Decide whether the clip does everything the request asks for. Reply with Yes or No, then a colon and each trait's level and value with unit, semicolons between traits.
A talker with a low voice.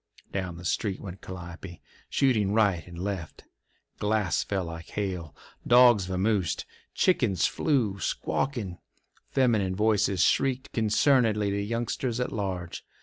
Yes: low, 100 Hz